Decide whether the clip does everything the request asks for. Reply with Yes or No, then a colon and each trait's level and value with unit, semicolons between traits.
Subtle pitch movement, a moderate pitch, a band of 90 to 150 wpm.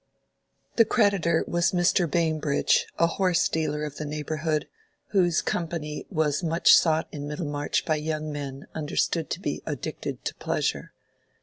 Yes: narrow, 2.2 semitones; medium, 155 Hz; average, 140 wpm